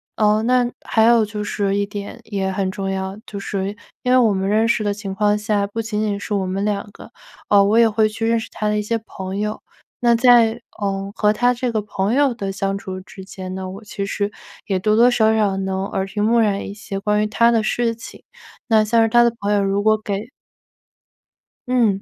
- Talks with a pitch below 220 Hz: Yes, high, 210 Hz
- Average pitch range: No, narrow, 2.3 semitones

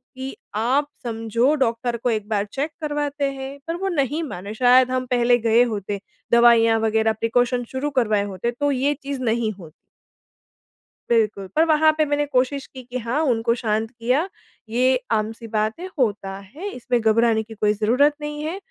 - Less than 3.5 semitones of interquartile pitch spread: No, average, 4.0 semitones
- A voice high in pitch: Yes, high, 240 Hz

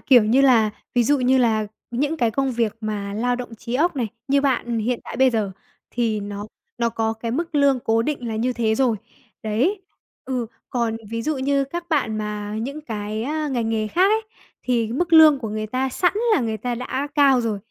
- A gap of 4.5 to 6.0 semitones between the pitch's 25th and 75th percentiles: No, average, 3.8 semitones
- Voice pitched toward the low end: No, high, 240 Hz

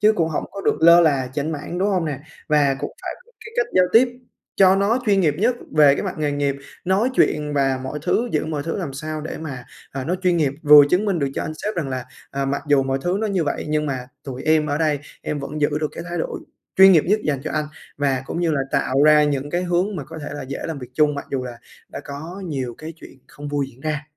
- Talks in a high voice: No, medium, 150 Hz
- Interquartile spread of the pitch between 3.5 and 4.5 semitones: Yes, average, 3.8 semitones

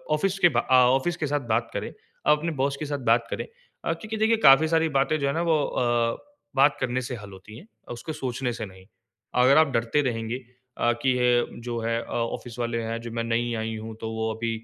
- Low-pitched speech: Yes, low, 120 Hz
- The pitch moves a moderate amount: Yes, average, 4.3 semitones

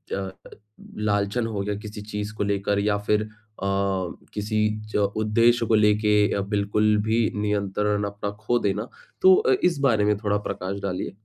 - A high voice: No, low, 105 Hz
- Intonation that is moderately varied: No, narrow, 1.0 semitones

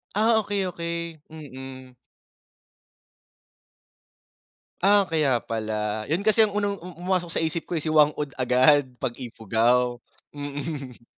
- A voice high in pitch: No, medium, 150 Hz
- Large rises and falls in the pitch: Yes, wide, 5.8 semitones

